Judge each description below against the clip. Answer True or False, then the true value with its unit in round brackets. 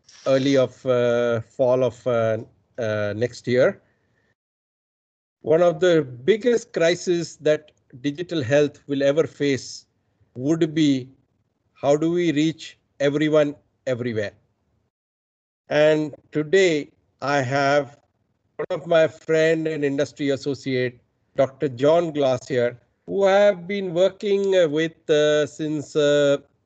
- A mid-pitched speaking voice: True (145 Hz)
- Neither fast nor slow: False (115 wpm)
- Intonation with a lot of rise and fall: False (4.4 semitones)